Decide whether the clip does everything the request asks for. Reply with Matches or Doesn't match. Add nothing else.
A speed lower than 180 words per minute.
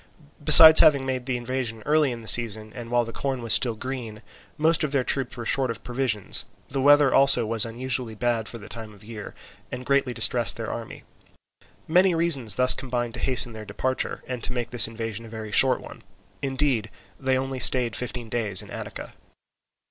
Doesn't match